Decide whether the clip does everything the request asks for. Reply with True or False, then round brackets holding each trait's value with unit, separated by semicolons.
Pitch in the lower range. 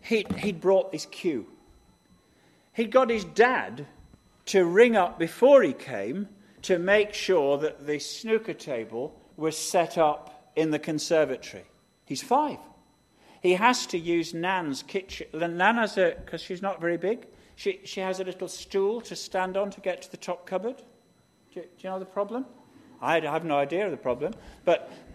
False (185 Hz)